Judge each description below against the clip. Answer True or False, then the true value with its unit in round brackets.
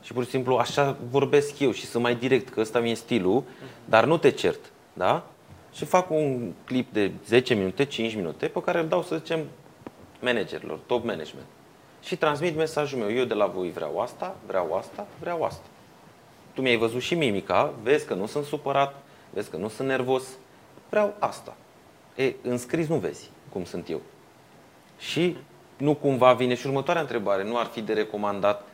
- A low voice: True (130 Hz)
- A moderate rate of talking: False (185 wpm)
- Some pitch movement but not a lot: True (4.2 semitones)